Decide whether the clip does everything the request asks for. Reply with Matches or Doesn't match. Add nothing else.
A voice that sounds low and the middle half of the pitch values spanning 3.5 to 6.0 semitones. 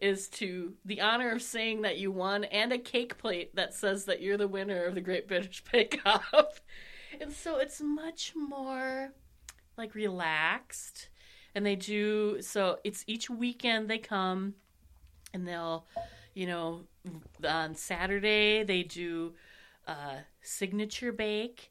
Doesn't match